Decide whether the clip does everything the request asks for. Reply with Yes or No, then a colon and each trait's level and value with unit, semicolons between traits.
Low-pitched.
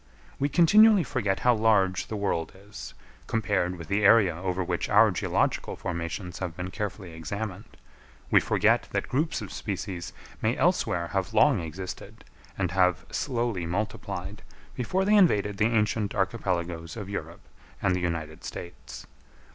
Yes: low, 100 Hz